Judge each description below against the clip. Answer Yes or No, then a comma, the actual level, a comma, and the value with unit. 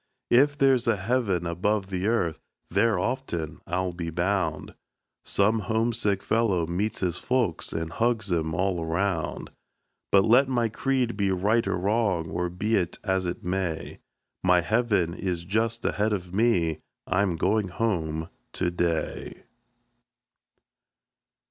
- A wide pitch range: No, average, 4.5 semitones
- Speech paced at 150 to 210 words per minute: No, slow, 135 wpm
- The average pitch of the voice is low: Yes, very low, 95 Hz